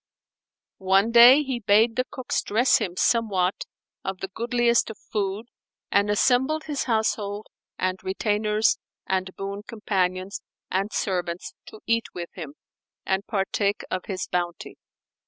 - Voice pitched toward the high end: Yes, high, 205 Hz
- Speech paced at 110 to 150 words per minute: Yes, slow, 135 wpm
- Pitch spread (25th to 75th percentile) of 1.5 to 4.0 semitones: Yes, average, 3.3 semitones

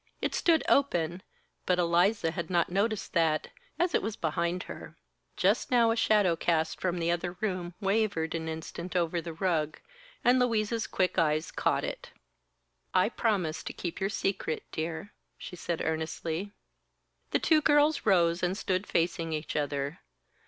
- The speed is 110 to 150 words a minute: No, average, 160 wpm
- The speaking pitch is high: No, medium, 175 Hz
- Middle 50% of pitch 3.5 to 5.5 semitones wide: Yes, average, 4.1 semitones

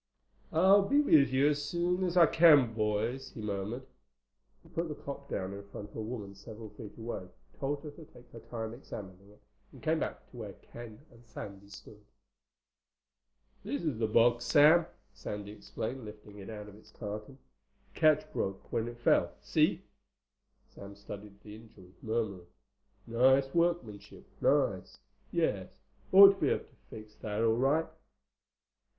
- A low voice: Yes, low, 115 Hz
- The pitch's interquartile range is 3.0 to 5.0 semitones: No, wide, 5.6 semitones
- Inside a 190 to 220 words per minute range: No, average, 165 wpm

